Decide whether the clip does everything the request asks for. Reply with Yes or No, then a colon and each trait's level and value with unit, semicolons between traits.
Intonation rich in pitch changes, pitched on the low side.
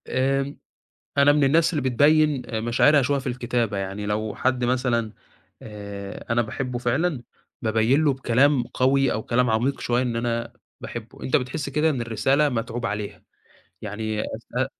No: average, 3.5 semitones; low, 125 Hz